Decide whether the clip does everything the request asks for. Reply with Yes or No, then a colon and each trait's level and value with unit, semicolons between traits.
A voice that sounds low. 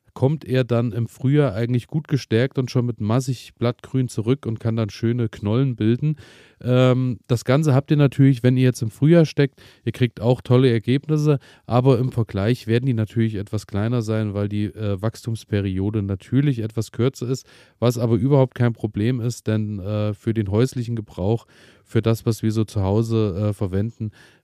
Yes: low, 115 Hz